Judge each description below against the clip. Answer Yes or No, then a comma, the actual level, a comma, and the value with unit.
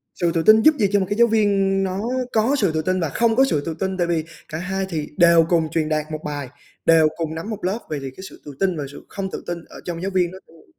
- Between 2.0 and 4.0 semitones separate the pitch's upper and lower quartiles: Yes, average, 3.6 semitones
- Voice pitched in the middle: Yes, medium, 175 Hz